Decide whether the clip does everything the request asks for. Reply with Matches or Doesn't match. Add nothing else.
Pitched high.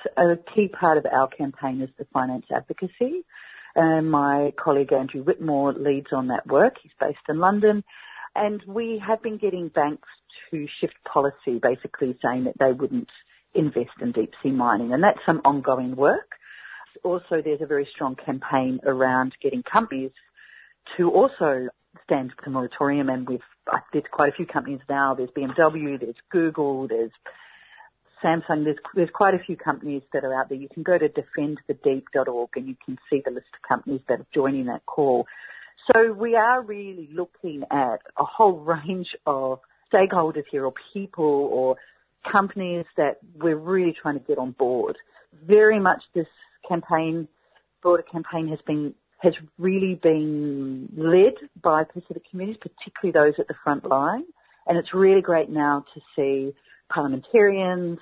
Doesn't match